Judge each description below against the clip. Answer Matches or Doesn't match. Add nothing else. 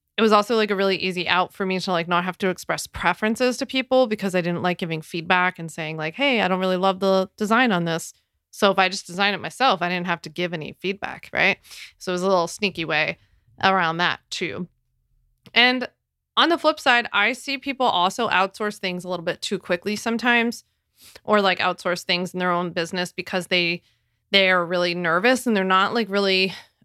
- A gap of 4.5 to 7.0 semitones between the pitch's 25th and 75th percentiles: Doesn't match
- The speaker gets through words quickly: Matches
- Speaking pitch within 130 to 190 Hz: Matches